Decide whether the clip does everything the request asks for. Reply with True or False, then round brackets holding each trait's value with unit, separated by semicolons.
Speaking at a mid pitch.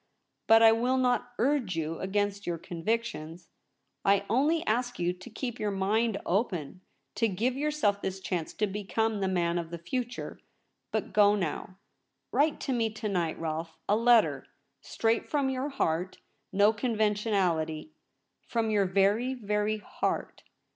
False (210 Hz)